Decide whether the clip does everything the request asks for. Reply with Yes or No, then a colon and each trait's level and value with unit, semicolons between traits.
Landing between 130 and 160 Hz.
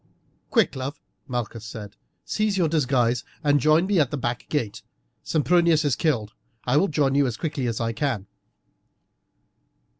Yes: medium, 140 Hz